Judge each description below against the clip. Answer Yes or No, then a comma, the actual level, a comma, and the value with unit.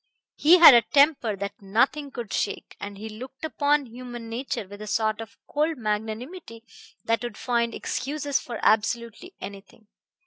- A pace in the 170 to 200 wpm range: No, average, 160 wpm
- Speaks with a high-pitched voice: Yes, high, 235 Hz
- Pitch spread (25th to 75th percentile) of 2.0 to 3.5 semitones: No, average, 4.5 semitones